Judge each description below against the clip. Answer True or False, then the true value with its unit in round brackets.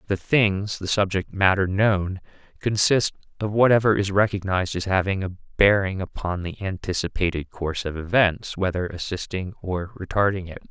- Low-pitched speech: True (95 Hz)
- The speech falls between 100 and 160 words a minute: True (145 wpm)